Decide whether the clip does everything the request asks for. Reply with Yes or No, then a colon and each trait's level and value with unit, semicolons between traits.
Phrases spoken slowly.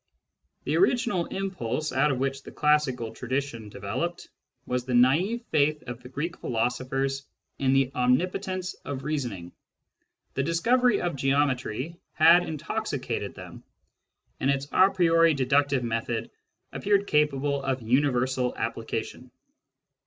Yes: slow, 125 wpm